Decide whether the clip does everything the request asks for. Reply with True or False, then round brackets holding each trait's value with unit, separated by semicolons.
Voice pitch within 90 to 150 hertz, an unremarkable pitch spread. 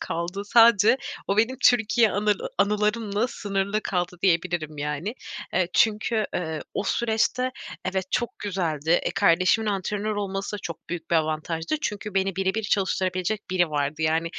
False (195 Hz; 3.8 semitones)